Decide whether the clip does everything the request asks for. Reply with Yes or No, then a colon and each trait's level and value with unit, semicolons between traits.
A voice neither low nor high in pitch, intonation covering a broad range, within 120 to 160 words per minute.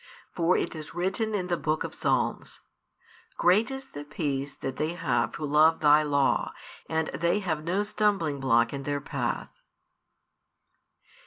No: medium, 160 Hz; average, 4.1 semitones; average, 150 wpm